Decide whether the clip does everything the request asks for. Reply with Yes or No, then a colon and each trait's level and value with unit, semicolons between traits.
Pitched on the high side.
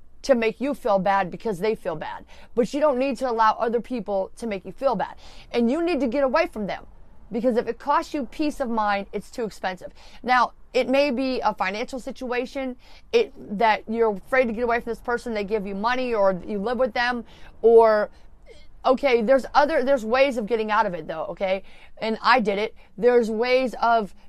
Yes: high, 240 Hz